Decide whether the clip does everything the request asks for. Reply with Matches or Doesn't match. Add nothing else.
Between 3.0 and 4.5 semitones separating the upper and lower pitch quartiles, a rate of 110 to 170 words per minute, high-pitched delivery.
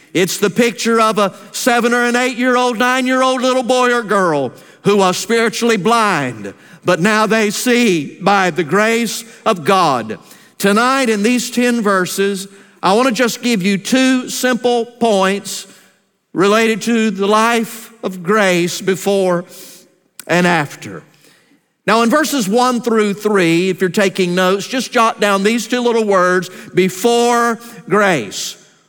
Matches